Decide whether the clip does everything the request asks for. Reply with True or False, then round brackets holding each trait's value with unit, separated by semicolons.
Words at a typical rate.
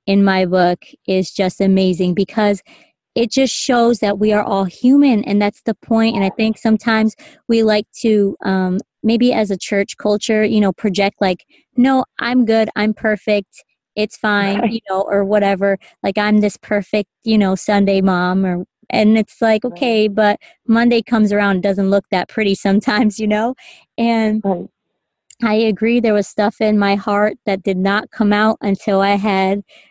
True (180 wpm)